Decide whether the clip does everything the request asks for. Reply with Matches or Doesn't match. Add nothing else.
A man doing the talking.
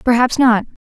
Doesn't match